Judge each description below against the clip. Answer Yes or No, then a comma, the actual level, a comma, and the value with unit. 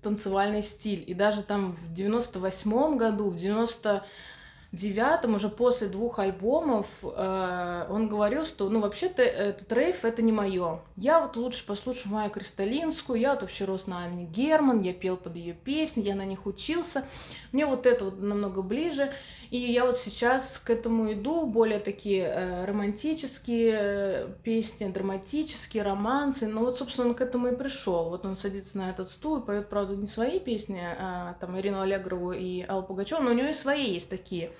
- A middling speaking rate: No, fast, 175 wpm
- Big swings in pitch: No, average, 4.2 semitones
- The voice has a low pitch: No, high, 210 Hz